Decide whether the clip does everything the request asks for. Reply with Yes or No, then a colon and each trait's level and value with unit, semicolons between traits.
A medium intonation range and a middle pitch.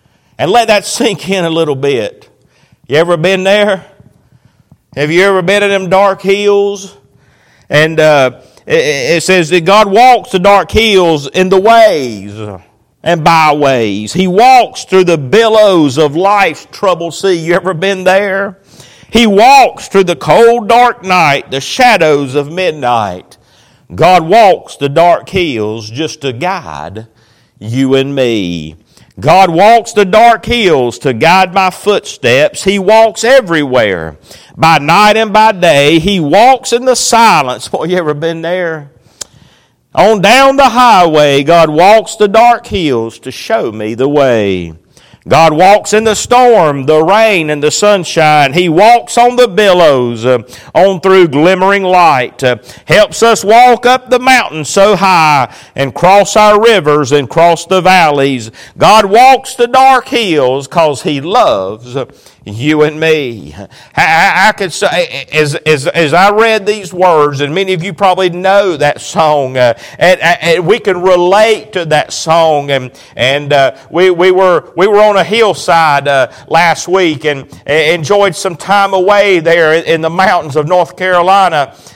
No: wide, 5.9 semitones; medium, 180 Hz